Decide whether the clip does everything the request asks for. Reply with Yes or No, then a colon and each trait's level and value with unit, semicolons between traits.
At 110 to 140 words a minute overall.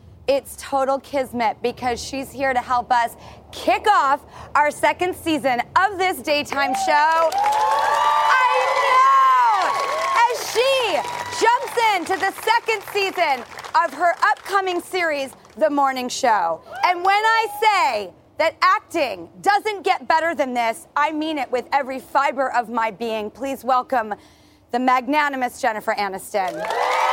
Yes: slow, 135 wpm